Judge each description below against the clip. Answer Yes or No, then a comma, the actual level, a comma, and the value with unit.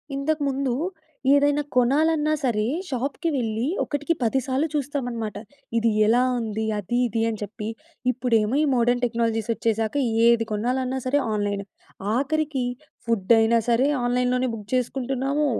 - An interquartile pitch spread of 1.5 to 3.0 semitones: No, average, 3.4 semitones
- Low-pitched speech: No, high, 245 Hz